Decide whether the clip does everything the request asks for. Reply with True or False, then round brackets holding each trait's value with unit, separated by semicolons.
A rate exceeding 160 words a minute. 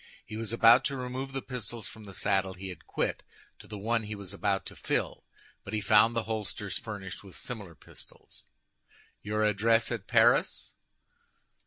True (175 wpm)